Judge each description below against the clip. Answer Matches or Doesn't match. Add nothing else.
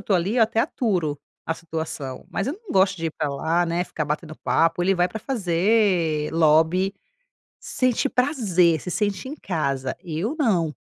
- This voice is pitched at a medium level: Matches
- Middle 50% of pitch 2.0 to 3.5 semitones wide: Doesn't match